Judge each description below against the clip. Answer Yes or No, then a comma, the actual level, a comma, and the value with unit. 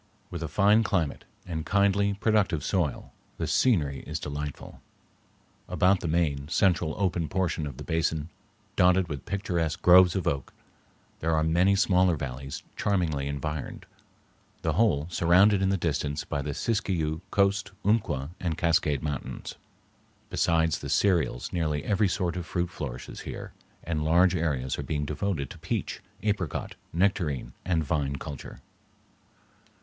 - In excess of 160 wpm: No, average, 145 wpm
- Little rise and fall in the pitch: No, average, 4.2 semitones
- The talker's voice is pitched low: Yes, very low, 85 Hz